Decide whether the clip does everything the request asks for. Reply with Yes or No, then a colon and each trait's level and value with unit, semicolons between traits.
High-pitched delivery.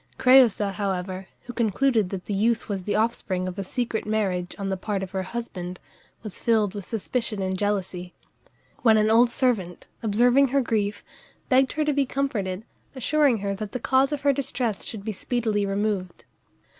Yes: high, 215 Hz